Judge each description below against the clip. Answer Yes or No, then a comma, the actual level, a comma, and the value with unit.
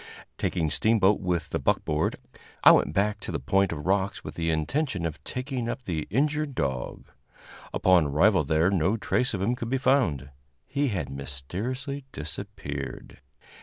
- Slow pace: No, average, 160 wpm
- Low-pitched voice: Yes, very low, 95 Hz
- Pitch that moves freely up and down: Yes, wide, 8.0 semitones